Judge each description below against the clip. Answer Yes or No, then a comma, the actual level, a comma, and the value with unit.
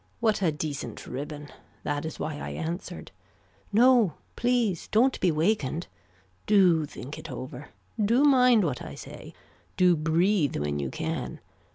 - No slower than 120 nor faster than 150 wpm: Yes, average, 145 wpm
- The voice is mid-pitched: Yes, medium, 170 Hz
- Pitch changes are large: Yes, wide, 6.4 semitones